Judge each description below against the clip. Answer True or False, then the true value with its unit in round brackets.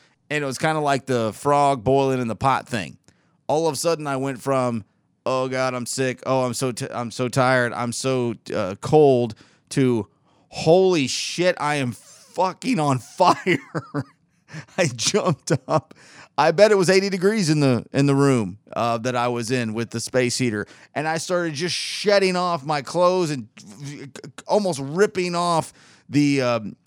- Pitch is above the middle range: False (140 Hz)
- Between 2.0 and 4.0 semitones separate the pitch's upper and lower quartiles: False (4.7 semitones)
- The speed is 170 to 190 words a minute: True (180 wpm)